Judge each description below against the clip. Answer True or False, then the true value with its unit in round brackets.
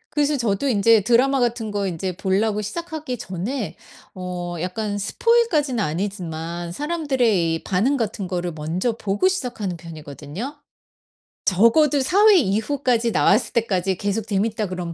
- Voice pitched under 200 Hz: False (210 Hz)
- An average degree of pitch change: False (6.0 semitones)